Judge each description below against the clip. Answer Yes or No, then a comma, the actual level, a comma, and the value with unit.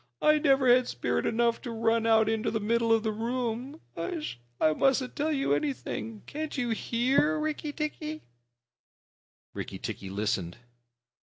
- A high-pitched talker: Yes, high, 240 Hz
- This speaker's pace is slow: No, average, 145 wpm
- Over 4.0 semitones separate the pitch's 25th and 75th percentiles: Yes, average, 4.9 semitones